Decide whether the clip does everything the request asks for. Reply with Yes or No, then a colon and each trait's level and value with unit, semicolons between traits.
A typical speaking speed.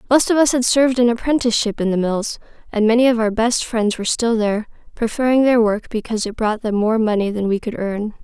No: fast, 235 wpm